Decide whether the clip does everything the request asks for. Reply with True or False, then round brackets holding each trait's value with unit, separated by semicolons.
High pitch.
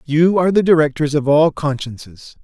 False (150 Hz)